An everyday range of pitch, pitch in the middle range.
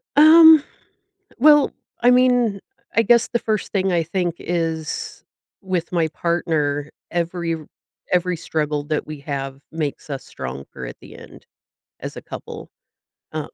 No: wide, 6.0 semitones; medium, 170 Hz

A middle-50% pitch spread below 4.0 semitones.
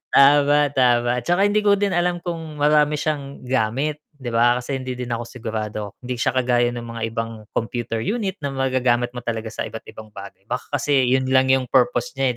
Yes: average, 3.6 semitones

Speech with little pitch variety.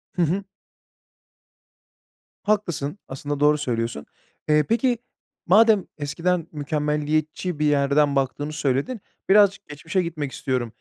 No: average, 4.1 semitones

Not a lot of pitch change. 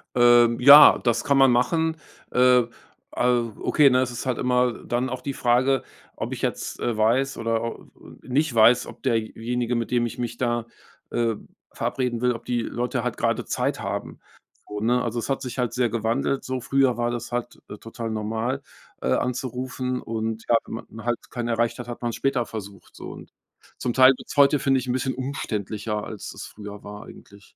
Yes: narrow, 1.9 semitones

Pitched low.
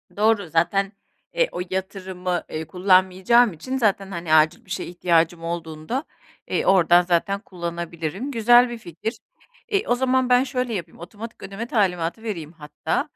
No: high, 190 Hz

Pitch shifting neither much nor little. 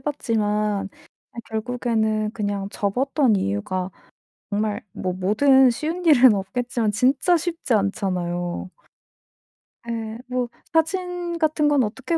No: wide, 5.7 semitones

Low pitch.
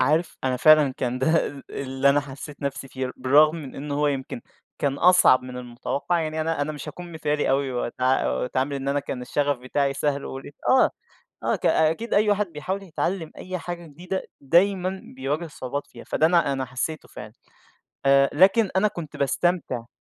No: medium, 145 Hz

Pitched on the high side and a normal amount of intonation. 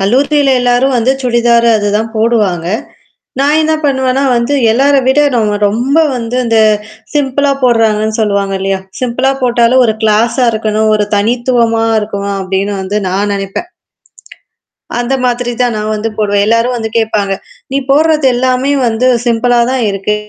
Yes: high, 235 Hz; average, 3.4 semitones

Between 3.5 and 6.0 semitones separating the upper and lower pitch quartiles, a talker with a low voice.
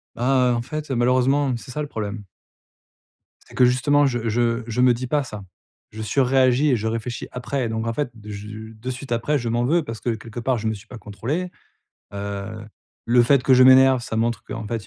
No: average, 2.8 semitones; low, 120 Hz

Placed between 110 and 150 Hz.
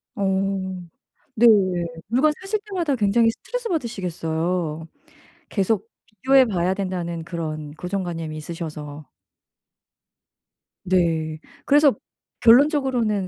No: high, 190 Hz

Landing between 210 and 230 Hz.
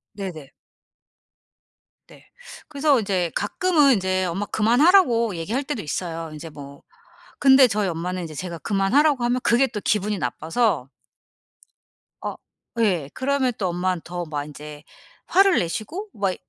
No: high, 200 Hz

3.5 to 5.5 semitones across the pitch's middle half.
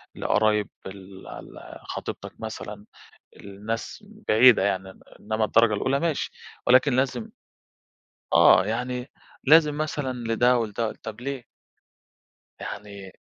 Yes: average, 4.0 semitones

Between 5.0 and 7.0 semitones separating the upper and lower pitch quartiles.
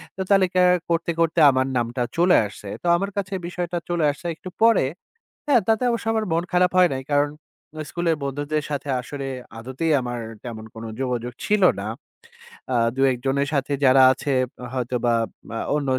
Yes: wide, 5.4 semitones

